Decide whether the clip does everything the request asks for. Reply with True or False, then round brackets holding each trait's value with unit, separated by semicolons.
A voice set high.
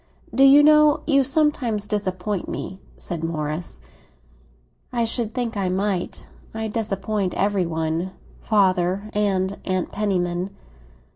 True (200 Hz)